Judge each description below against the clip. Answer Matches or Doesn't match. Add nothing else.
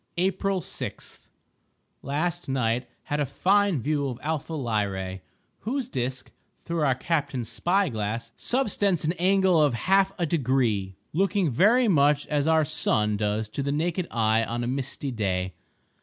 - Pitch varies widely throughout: Matches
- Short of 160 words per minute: Matches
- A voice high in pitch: Doesn't match